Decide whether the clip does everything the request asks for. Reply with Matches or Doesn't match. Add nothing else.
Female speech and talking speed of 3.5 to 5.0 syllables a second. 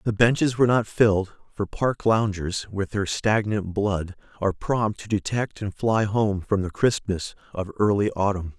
Doesn't match